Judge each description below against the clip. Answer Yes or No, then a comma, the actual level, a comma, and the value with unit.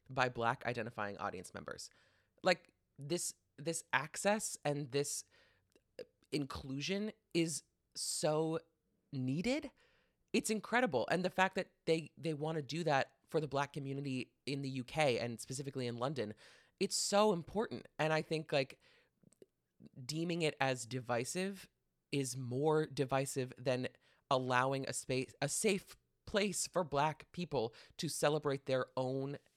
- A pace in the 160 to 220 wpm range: No, slow, 135 wpm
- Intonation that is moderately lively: Yes, average, 4.3 semitones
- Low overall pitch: No, medium, 145 Hz